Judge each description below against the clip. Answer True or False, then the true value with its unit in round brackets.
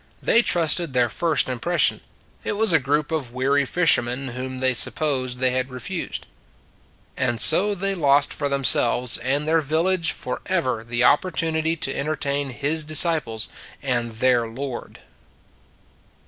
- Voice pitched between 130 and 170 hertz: True (140 Hz)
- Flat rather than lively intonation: False (4.1 semitones)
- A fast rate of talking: False (145 wpm)